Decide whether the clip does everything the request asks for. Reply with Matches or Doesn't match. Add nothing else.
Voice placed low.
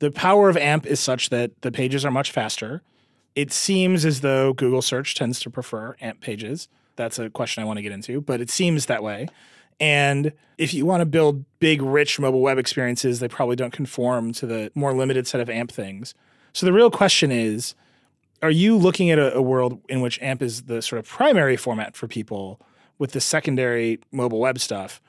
Matches